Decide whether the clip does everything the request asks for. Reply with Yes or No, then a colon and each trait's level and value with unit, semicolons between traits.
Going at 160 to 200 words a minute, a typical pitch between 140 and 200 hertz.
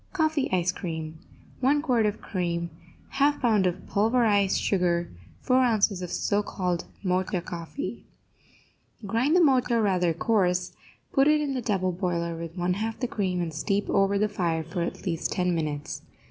Yes: average, 165 wpm; high, 190 Hz